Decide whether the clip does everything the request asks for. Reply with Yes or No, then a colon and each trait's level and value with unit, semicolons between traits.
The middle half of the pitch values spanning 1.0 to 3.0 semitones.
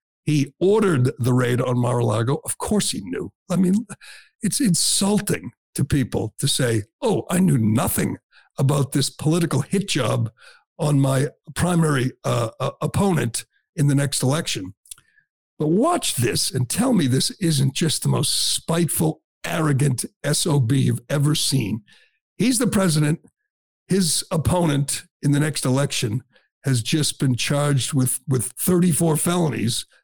No: average, 4.6 semitones